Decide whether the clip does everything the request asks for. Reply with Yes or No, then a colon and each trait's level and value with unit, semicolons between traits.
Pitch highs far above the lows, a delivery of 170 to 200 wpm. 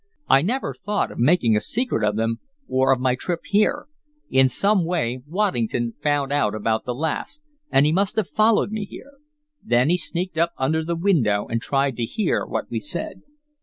Yes: wide, 7.7 semitones; average, 195 wpm